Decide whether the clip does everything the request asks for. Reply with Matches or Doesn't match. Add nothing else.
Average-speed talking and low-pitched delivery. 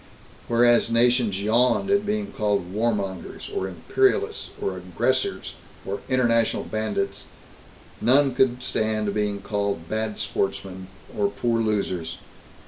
Doesn't match